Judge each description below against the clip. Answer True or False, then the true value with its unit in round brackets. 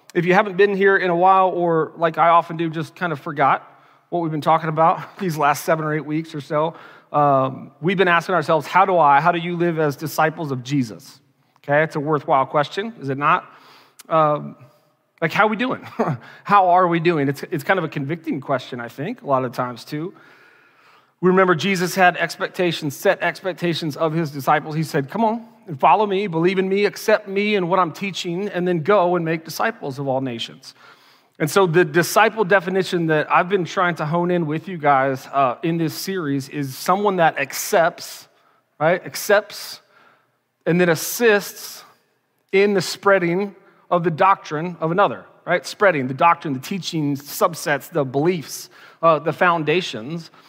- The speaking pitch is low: False (170 Hz)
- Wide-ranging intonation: False (3.7 semitones)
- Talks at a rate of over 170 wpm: True (195 wpm)